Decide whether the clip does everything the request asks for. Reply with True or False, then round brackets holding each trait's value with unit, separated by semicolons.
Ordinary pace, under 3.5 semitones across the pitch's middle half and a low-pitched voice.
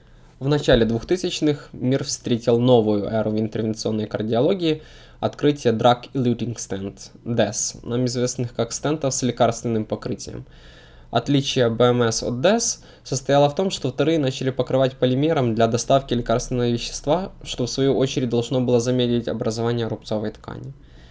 True (135 wpm; 2.9 semitones; 120 Hz)